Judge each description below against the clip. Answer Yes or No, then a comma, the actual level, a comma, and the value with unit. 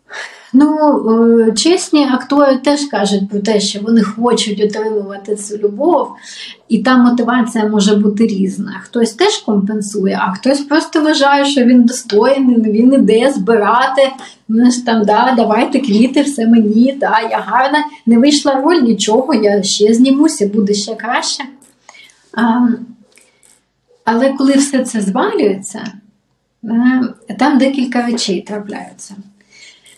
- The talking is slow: No, average, 125 wpm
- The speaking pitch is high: Yes, high, 230 Hz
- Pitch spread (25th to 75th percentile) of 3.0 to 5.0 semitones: Yes, average, 4.2 semitones